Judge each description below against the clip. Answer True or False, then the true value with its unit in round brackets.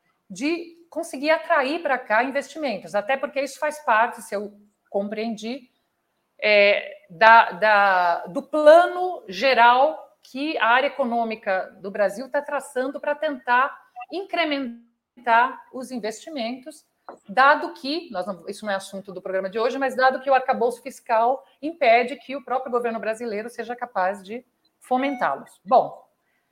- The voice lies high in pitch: True (250 Hz)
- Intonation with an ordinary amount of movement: True (4.8 semitones)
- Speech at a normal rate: True (140 wpm)